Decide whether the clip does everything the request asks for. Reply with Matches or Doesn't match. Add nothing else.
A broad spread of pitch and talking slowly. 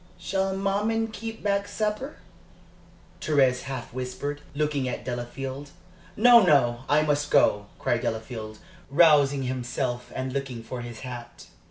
Matches